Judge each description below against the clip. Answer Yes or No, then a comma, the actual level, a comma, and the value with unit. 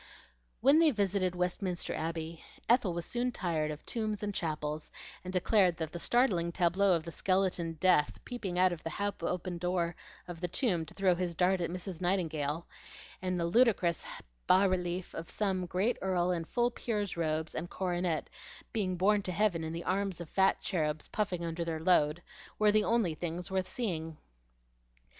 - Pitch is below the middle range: No, medium, 180 Hz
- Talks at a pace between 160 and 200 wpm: Yes, average, 180 wpm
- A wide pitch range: No, average, 2.8 semitones